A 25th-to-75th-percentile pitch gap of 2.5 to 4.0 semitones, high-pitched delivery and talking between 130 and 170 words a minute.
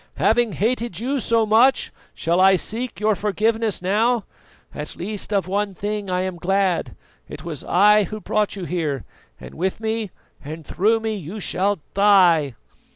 Yes: average, 3.4 semitones; high, 200 Hz; average, 160 wpm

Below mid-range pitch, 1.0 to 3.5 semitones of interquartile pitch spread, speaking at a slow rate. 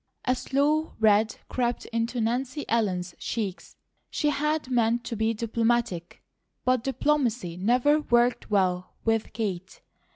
No: high, 230 Hz; average, 3.1 semitones; slow, 125 wpm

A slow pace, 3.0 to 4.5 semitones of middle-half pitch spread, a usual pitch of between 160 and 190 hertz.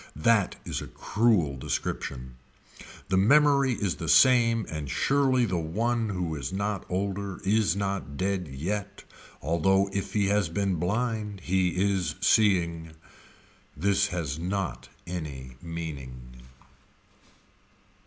No: slow, 120 wpm; average, 4.2 semitones; very low, 95 Hz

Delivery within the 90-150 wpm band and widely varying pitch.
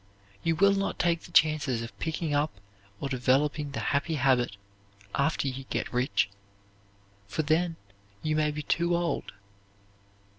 No: average, 145 wpm; average, 3.4 semitones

